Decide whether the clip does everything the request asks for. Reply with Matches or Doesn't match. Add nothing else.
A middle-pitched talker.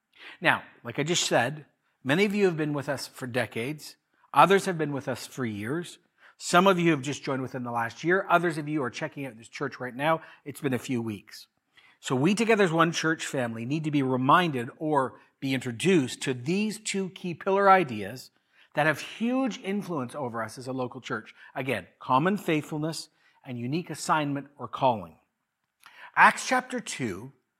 Matches